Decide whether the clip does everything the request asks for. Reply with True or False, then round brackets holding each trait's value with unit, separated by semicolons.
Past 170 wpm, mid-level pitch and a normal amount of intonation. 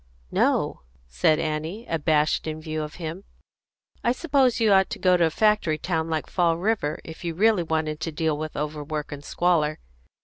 True (180 wpm; 160 Hz; 3.0 semitones)